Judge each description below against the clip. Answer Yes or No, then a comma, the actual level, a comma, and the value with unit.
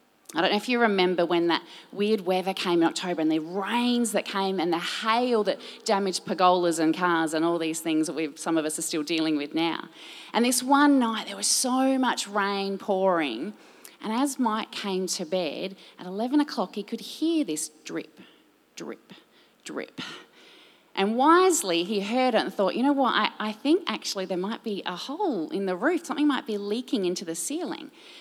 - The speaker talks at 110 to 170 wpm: No, average, 200 wpm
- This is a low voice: No, high, 200 Hz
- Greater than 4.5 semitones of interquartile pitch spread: Yes, wide, 5.4 semitones